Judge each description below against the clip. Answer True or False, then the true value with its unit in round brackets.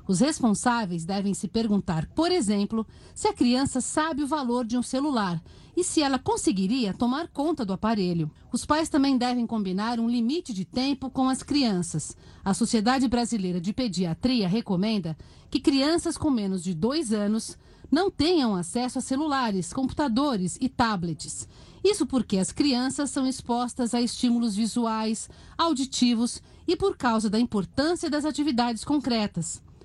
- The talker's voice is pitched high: True (245 Hz)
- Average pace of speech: True (150 wpm)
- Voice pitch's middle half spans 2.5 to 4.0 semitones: False (5.2 semitones)